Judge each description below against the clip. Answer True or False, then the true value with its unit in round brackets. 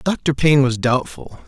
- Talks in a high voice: False (140 Hz)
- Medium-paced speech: True (160 wpm)